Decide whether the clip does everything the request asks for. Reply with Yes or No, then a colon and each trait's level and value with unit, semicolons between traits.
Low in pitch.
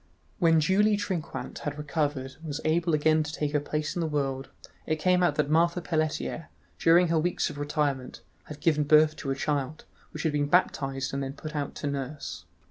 No: medium, 150 Hz